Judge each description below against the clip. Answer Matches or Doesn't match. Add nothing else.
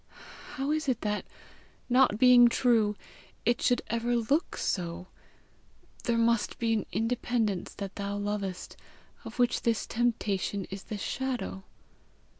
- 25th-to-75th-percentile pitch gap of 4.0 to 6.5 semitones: Doesn't match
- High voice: Matches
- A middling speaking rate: Doesn't match